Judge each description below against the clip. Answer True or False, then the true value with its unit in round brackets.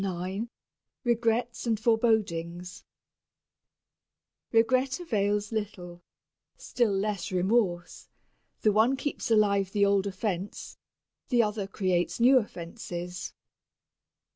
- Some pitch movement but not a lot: True (3.8 semitones)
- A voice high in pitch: True (205 Hz)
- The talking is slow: True (90 wpm)